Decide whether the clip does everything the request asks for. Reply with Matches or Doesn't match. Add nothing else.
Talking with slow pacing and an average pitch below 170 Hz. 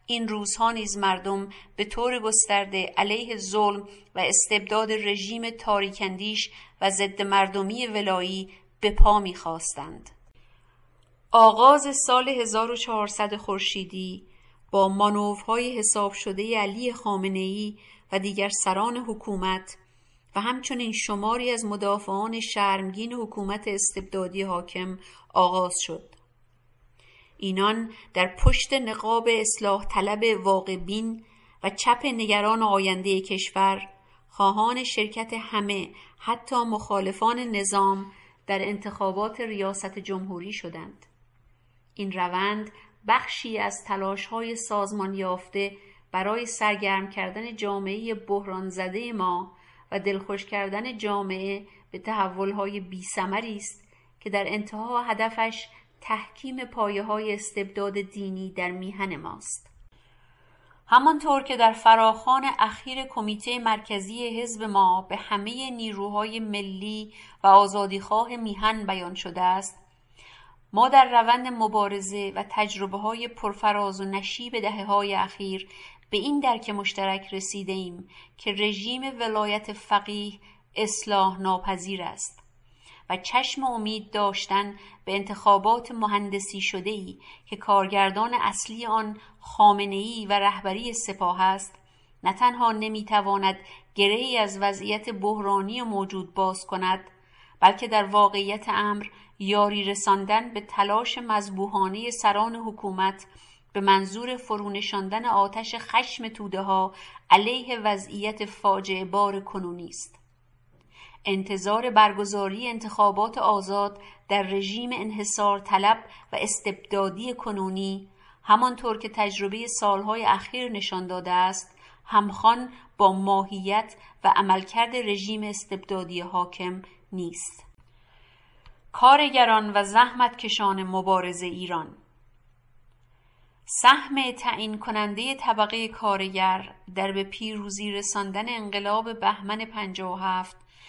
Doesn't match